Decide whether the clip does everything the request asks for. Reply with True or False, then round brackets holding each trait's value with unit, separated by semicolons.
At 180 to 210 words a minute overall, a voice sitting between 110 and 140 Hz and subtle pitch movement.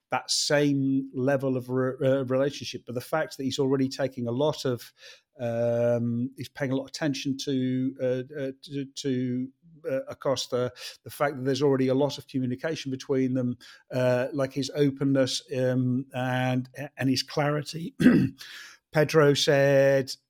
False (155 wpm; 135 Hz; 1.7 semitones)